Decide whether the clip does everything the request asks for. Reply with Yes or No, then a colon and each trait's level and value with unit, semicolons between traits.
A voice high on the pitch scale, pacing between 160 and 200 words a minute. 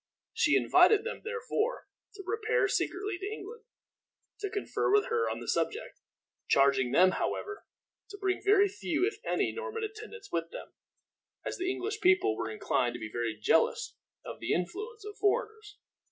Yes: very high, 415 Hz; average, 165 wpm